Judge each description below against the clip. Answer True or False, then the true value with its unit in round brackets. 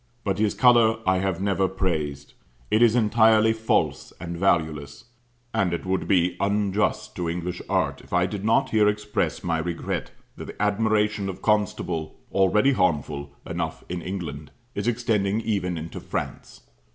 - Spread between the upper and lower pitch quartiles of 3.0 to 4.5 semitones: True (3.5 semitones)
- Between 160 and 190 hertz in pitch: False (95 Hz)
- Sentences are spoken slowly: False (155 wpm)